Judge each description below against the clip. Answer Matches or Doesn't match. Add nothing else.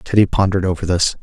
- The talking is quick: Doesn't match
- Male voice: Matches